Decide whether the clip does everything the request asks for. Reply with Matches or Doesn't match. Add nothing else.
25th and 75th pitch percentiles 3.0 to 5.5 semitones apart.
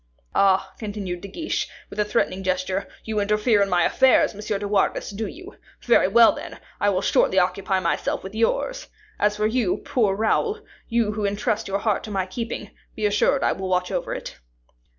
Doesn't match